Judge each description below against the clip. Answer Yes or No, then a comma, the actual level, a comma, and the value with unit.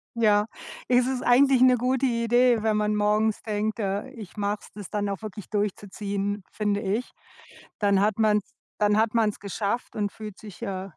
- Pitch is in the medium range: No, high, 210 Hz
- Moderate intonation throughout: No, narrow, 2.1 semitones